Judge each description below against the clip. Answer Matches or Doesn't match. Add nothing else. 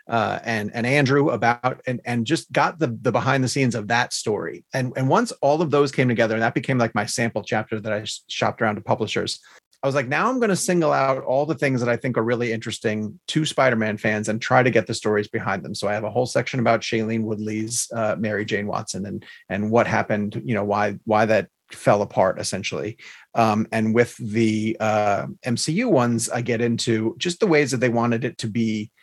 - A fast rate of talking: Matches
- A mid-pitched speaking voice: Doesn't match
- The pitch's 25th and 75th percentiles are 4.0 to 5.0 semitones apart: Doesn't match